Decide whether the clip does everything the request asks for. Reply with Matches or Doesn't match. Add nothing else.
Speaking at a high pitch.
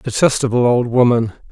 Doesn't match